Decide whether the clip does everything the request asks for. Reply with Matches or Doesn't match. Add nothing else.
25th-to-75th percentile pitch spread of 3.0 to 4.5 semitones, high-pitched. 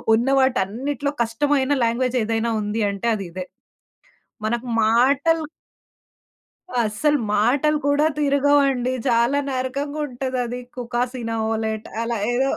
Matches